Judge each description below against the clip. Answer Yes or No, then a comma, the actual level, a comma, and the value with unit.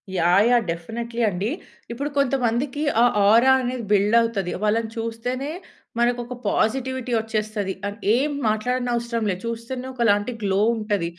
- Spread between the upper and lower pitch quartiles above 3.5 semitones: No, average, 2.9 semitones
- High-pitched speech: Yes, high, 230 Hz